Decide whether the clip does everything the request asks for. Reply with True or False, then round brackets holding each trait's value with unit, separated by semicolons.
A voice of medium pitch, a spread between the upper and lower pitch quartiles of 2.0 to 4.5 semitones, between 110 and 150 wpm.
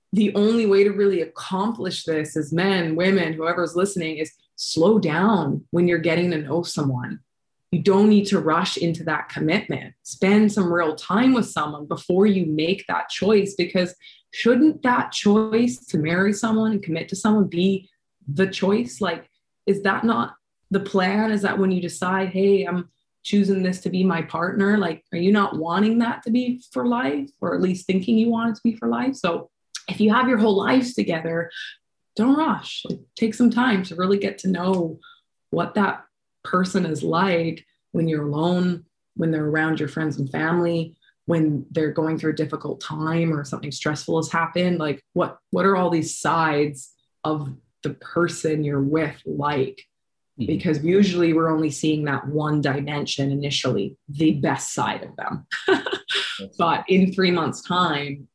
False (175 Hz; 4.0 semitones; 175 wpm)